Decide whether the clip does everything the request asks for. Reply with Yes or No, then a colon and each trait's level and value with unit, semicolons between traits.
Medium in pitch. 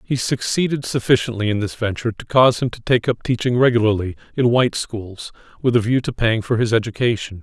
No: low, 115 Hz